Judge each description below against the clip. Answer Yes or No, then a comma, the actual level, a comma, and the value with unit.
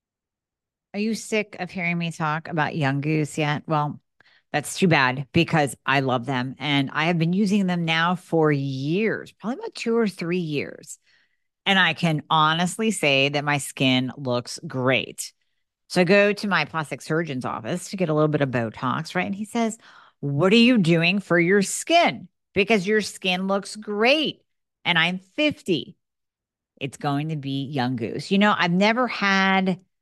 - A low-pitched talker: No, medium, 170 Hz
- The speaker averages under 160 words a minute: No, average, 180 wpm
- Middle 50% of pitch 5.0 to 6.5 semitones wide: Yes, wide, 5.5 semitones